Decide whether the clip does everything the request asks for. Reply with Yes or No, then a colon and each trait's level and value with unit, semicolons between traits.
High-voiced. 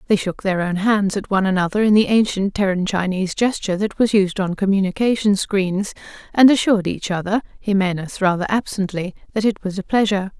Yes: high, 200 Hz